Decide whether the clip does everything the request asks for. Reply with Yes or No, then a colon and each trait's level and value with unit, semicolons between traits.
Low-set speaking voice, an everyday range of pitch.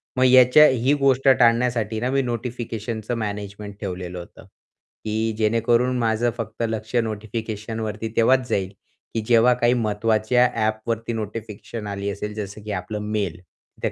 No: low, 110 Hz; narrow, 2.3 semitones